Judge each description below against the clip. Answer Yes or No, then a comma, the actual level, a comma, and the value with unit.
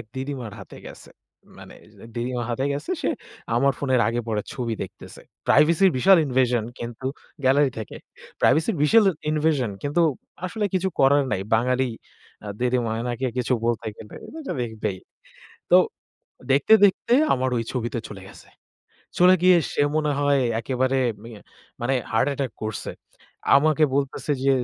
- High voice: No, low, 130 Hz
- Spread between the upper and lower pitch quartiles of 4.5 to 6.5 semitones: No, average, 3.5 semitones